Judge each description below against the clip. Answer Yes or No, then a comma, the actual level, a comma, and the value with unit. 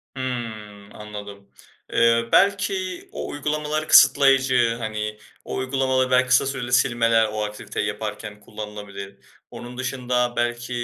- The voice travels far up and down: No, average, 3.5 semitones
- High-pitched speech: No, low, 120 Hz